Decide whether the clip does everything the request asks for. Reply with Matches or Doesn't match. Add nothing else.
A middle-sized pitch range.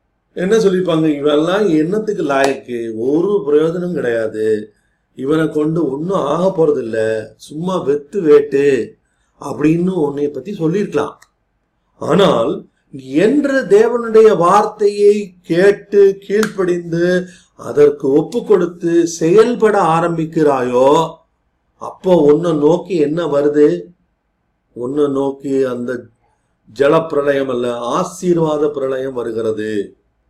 Doesn't match